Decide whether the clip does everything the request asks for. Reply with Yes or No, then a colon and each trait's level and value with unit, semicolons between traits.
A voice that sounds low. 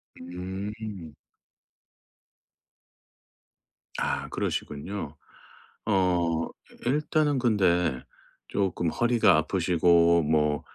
Yes: very low, 90 Hz